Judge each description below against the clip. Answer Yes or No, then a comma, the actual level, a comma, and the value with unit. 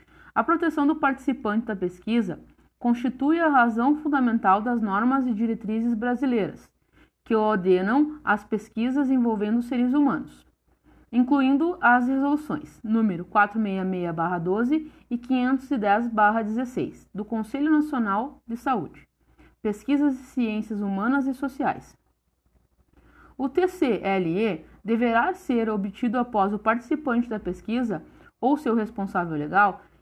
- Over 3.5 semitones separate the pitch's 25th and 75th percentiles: Yes, average, 4.3 semitones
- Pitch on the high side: Yes, high, 235 Hz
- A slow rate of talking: Yes, slow, 110 wpm